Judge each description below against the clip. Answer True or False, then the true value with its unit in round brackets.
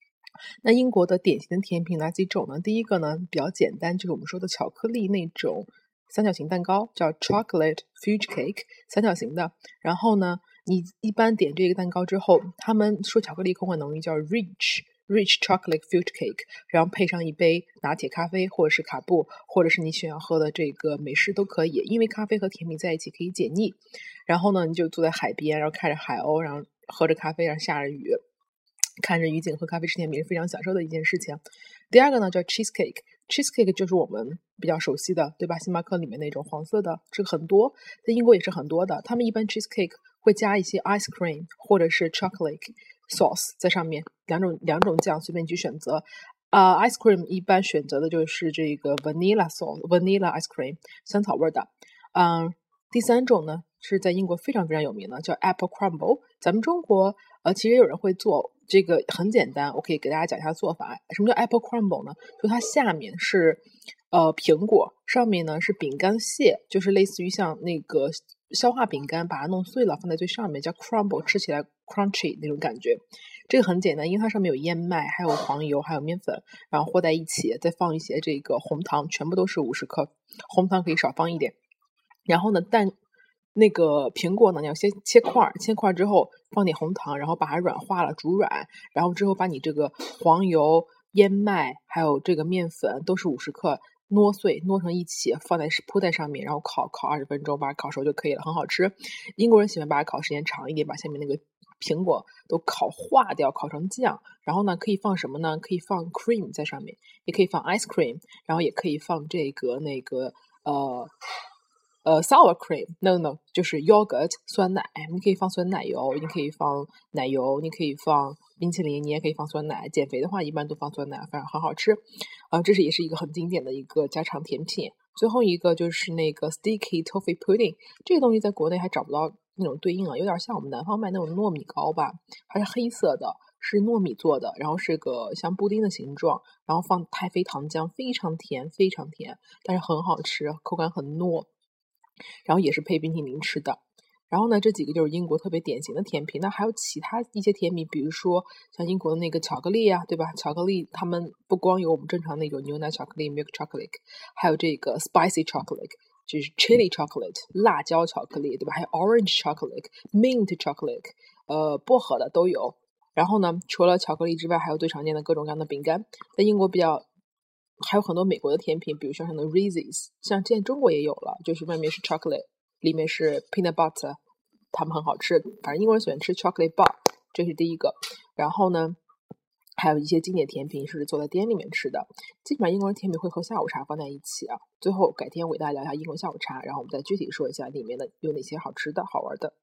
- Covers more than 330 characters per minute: True (395 characters per minute)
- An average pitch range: True (4.9 semitones)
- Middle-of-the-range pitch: True (180 Hz)